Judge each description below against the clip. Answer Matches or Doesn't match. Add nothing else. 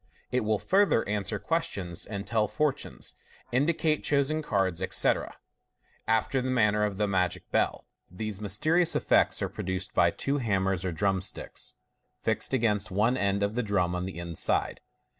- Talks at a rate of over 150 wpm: Matches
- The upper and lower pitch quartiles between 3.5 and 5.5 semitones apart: Matches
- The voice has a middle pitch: Doesn't match